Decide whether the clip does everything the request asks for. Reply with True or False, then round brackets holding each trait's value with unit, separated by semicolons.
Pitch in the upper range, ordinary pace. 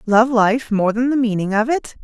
False (230 Hz; 235 wpm)